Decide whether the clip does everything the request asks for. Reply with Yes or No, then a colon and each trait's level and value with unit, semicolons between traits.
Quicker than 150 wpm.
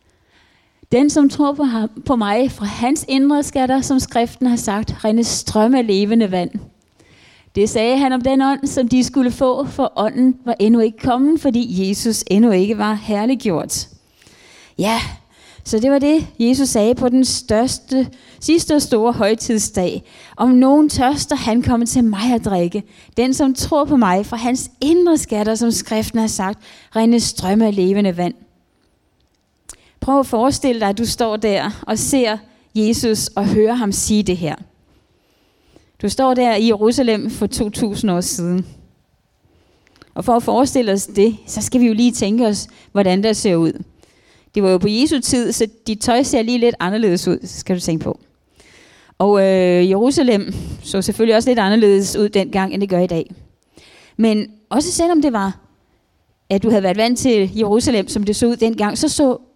Yes: average, 175 wpm